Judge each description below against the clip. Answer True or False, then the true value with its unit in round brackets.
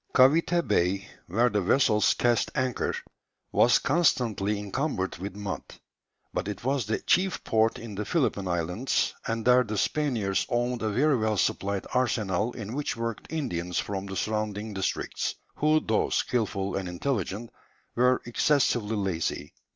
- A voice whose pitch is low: True (110 Hz)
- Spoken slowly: False (145 wpm)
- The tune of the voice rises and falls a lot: False (4.3 semitones)